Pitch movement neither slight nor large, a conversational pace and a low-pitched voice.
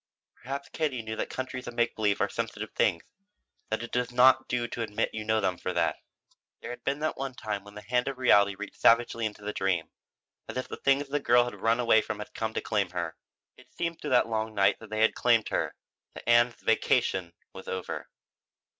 No: average, 3.1 semitones; fast, 225 wpm; low, 115 Hz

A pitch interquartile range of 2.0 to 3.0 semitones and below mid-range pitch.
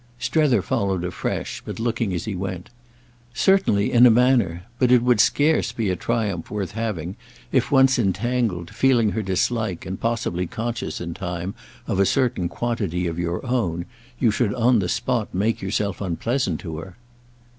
No: average, 5.0 semitones; low, 105 Hz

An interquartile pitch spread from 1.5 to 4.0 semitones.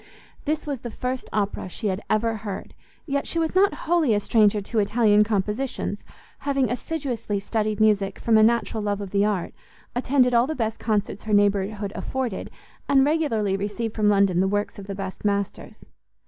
Yes: average, 3.6 semitones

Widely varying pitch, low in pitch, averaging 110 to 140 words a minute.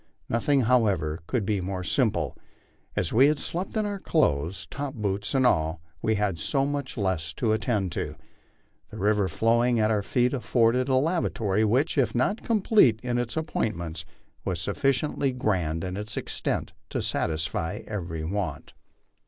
No: wide, 6.0 semitones; low, 110 Hz; average, 160 wpm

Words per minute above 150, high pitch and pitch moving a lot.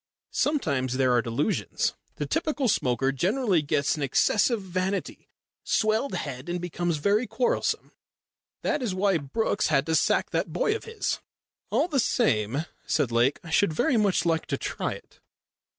No: average, 160 wpm; medium, 175 Hz; wide, 8.0 semitones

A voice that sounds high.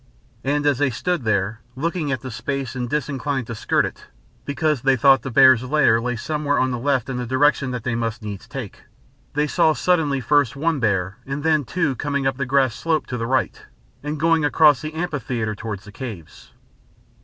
No: low, 135 Hz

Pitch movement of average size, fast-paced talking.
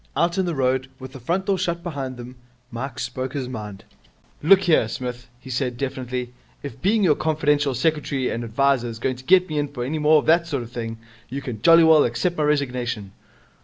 Yes: average, 4.1 semitones; fast, 215 wpm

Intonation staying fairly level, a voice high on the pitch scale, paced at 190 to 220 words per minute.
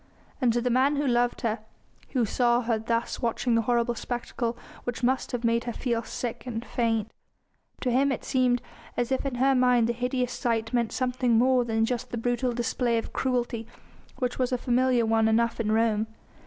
Yes: narrow, 1.6 semitones; high, 240 Hz; average, 200 wpm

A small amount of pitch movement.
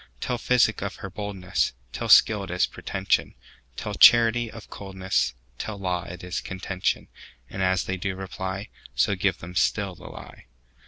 Yes: narrow, 2.2 semitones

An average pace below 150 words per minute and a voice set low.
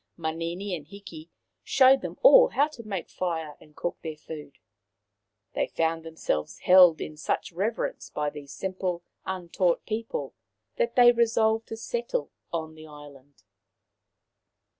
No: average, 140 wpm; medium, 175 Hz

